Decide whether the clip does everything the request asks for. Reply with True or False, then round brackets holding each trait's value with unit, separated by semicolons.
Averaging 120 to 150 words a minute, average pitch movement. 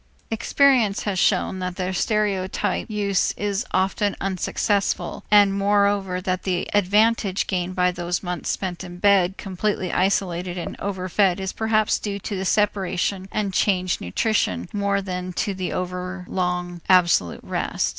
False (140 wpm; 2.0 semitones)